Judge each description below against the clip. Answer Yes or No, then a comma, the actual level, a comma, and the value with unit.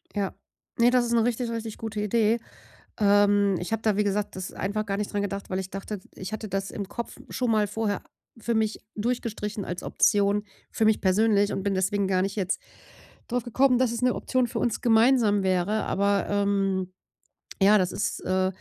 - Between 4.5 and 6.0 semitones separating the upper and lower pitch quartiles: No, narrow, 2.4 semitones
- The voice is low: No, high, 205 Hz